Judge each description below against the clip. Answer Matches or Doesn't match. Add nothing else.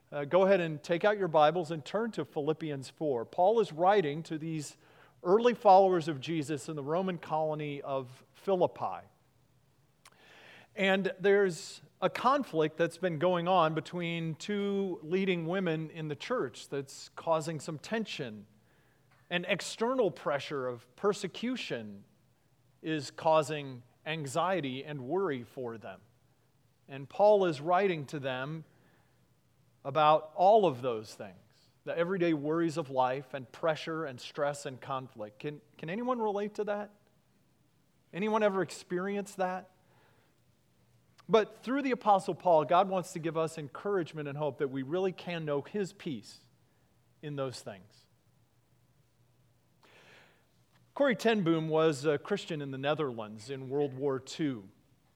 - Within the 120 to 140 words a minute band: Matches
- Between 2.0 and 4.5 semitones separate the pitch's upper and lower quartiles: Doesn't match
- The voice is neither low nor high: Matches